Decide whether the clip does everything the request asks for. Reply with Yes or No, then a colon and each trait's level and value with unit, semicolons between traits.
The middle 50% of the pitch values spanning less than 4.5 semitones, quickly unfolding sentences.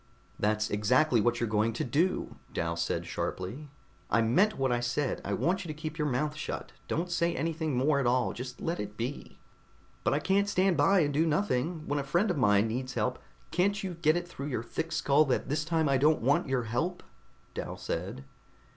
No: wide, 5.4 semitones; fast, 215 wpm